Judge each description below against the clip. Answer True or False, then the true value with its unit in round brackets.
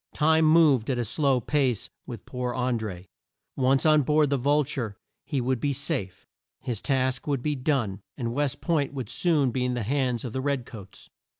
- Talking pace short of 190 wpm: False (200 wpm)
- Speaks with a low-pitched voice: True (130 Hz)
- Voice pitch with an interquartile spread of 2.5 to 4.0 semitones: True (3.0 semitones)